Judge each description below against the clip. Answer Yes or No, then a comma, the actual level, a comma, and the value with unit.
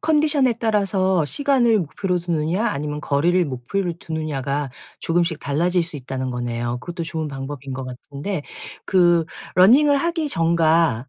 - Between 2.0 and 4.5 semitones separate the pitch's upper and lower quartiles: No, wide, 5.5 semitones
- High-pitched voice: No, medium, 165 Hz